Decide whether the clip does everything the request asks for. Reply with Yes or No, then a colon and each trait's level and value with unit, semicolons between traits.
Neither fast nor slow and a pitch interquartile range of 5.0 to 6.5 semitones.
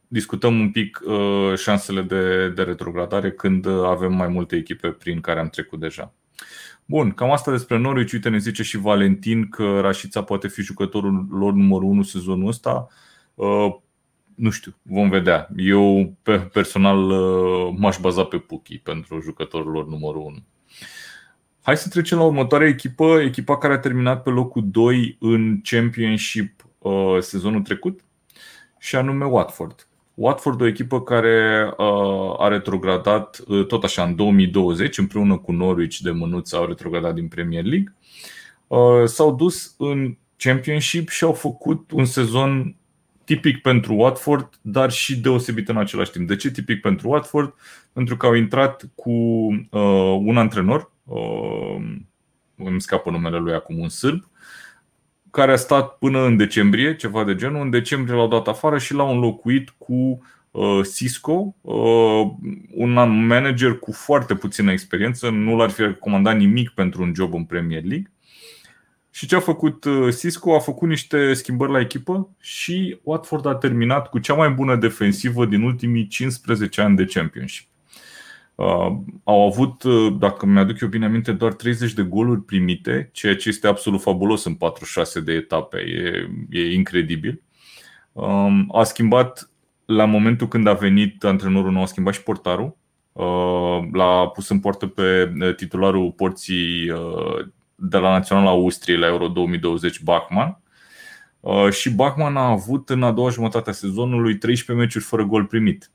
Yes: average, 150 wpm; average, 5.3 semitones